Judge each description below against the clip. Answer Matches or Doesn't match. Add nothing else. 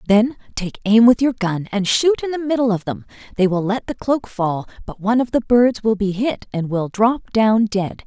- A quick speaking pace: Matches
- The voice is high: Matches